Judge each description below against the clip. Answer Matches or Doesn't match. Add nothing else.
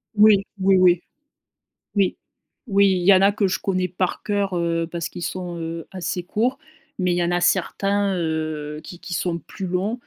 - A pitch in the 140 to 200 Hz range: Matches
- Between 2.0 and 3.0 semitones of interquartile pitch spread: Matches